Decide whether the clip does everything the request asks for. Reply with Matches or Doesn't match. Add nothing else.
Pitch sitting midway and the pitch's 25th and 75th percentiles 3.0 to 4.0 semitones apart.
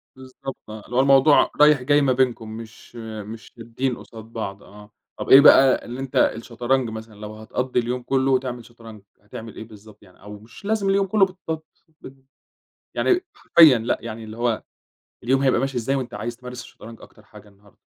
Doesn't match